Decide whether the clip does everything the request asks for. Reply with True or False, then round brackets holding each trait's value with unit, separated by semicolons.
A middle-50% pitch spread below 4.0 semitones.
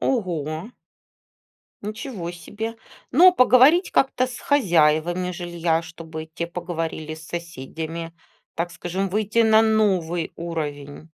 False (5.1 semitones)